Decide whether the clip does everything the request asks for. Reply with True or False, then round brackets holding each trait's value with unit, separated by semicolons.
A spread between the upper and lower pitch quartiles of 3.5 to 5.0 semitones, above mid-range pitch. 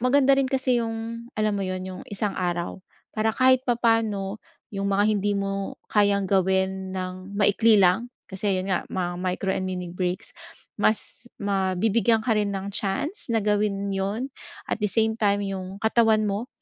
False (2.8 semitones; 200 Hz)